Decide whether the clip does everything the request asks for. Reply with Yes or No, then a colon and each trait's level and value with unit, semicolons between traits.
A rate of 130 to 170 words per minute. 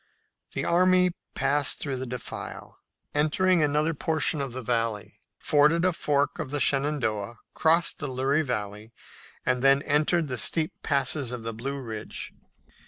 Yes: average, 150 wpm